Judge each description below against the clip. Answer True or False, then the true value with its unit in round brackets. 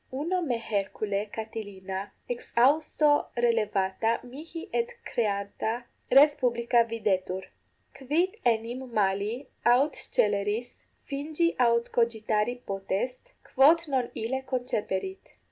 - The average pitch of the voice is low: False (235 Hz)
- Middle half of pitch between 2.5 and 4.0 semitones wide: False (4.5 semitones)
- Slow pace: True (95 wpm)